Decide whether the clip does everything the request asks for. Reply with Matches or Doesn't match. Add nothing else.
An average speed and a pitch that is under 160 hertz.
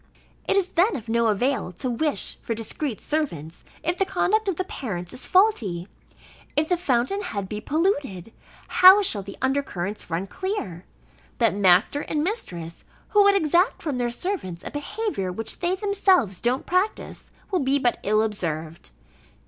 Doesn't match